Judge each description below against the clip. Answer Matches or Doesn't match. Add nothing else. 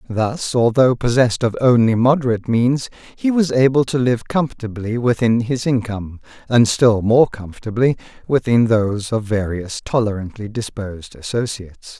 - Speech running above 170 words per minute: Doesn't match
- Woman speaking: Doesn't match